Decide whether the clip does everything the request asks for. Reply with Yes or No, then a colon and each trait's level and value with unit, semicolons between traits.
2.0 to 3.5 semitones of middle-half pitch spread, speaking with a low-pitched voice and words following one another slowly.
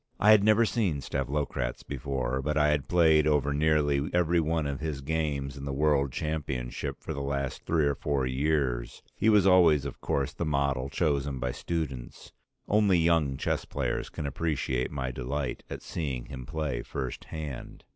No: average, 2.7 semitones; very low, 70 Hz; average, 175 wpm